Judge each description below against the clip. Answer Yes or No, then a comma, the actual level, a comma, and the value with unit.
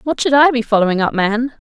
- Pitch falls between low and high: No, high, 240 Hz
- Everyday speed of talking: No, fast, 250 wpm